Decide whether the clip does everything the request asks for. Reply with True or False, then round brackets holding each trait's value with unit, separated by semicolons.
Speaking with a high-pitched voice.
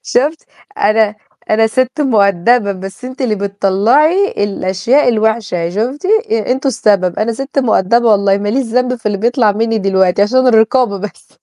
True (220 Hz)